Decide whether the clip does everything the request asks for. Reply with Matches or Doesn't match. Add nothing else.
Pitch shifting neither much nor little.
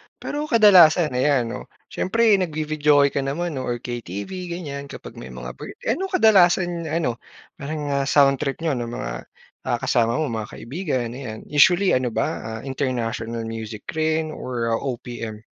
Doesn't match